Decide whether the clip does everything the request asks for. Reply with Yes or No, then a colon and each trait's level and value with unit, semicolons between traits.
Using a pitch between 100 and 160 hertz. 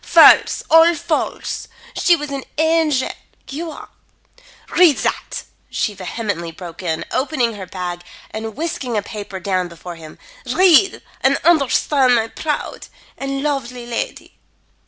No: very high, 250 Hz